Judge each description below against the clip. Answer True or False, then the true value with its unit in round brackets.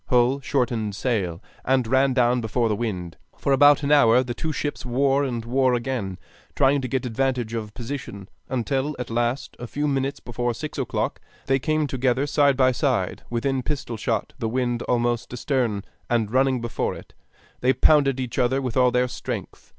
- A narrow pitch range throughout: True (2.3 semitones)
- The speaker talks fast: False (180 wpm)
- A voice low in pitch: True (125 Hz)